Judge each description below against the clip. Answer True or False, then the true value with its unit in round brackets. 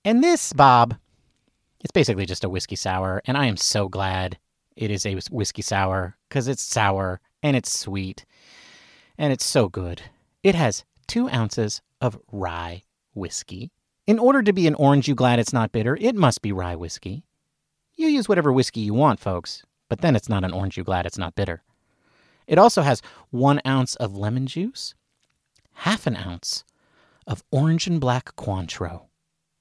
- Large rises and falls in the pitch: True (6.8 semitones)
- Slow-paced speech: False (175 wpm)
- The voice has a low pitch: True (115 Hz)